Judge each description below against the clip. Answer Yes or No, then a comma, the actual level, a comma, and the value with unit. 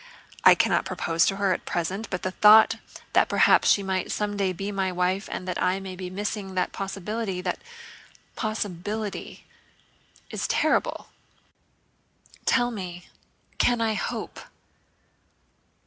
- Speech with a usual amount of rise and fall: No, narrow, 2.3 semitones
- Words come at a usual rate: No, slow, 130 wpm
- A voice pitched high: Yes, high, 195 Hz